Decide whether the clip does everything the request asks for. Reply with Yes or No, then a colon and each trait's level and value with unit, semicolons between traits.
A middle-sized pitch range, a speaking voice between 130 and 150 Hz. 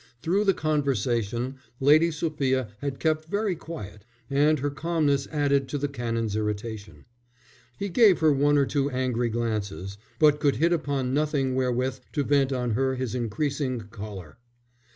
Yes: average, 4.2 semitones; low, 135 Hz